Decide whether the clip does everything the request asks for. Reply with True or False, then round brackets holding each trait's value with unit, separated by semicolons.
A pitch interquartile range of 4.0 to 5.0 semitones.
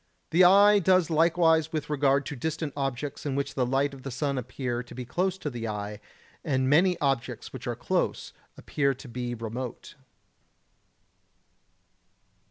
True (4.3 semitones)